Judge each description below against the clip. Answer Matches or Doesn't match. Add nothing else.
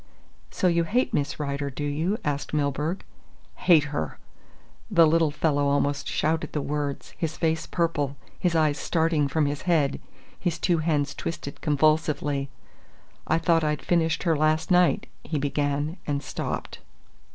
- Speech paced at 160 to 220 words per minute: Doesn't match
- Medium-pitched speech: Matches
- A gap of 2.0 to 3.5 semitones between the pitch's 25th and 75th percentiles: Matches